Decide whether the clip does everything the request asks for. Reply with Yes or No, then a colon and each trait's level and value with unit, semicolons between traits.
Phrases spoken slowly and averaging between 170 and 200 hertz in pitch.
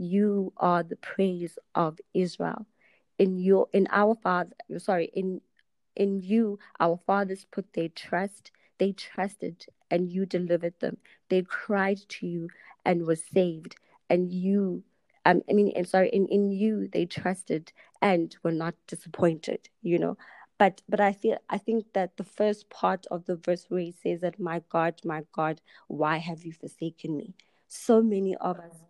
No: average, 170 wpm; medium, 185 Hz